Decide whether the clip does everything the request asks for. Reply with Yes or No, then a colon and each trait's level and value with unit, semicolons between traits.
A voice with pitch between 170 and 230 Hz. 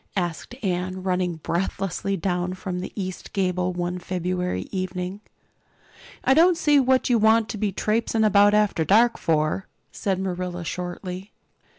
Yes: medium, 185 Hz